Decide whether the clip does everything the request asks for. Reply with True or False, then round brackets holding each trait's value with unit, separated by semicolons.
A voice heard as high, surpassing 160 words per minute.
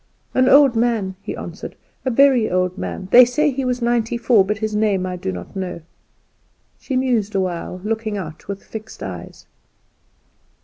True (220 Hz; 175 wpm)